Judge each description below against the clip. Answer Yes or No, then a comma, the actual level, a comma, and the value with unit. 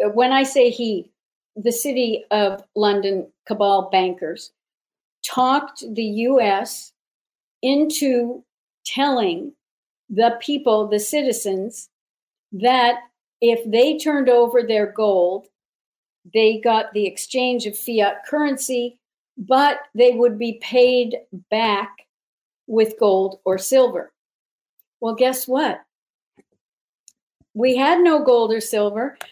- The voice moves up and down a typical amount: Yes, average, 3.4 semitones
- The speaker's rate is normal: No, slow, 105 wpm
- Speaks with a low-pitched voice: No, high, 235 Hz